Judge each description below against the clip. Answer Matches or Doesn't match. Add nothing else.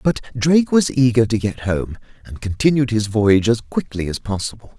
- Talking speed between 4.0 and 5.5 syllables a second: Matches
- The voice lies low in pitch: Matches